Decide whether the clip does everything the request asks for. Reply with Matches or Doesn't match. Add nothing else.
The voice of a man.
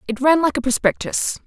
Doesn't match